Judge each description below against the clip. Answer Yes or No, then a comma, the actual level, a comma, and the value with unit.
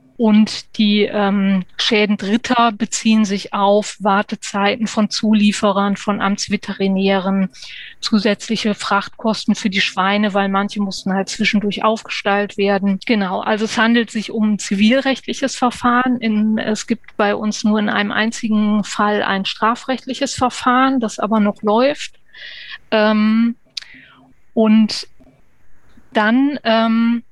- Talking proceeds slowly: Yes, slow, 120 wpm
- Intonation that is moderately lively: No, narrow, 1.9 semitones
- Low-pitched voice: No, high, 215 Hz